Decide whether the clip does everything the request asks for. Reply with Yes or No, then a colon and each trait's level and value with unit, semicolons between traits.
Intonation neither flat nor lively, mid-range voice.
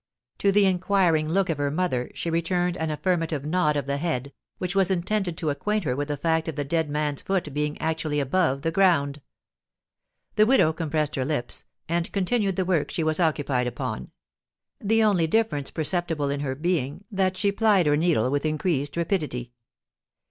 Yes: average, 4.1 semitones; medium, 160 Hz